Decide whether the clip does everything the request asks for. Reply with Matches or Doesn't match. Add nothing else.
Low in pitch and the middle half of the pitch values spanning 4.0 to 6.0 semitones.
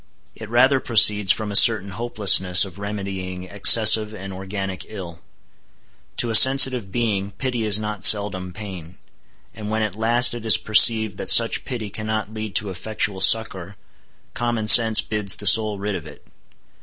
Doesn't match